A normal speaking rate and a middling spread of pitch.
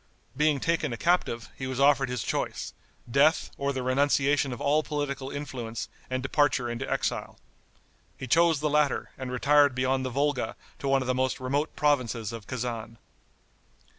No: average, 165 wpm; narrow, 2.3 semitones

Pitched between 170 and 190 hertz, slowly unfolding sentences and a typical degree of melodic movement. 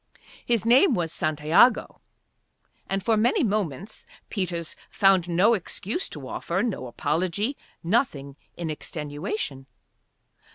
No: medium, 185 Hz; slow, 110 wpm; wide, 6.1 semitones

